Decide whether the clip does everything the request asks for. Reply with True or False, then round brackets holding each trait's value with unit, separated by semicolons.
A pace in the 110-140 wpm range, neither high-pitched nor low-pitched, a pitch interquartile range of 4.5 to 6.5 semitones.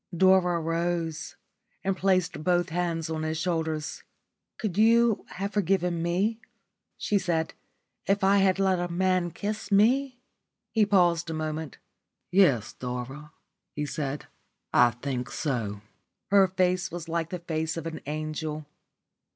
False (135 wpm; 175 Hz; 3.4 semitones)